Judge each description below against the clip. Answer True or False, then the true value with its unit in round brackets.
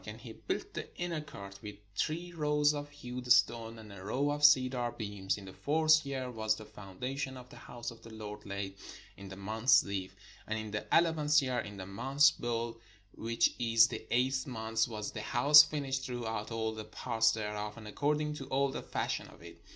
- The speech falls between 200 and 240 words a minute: True (205 wpm)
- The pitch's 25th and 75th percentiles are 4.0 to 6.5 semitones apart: True (4.5 semitones)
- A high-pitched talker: False (120 Hz)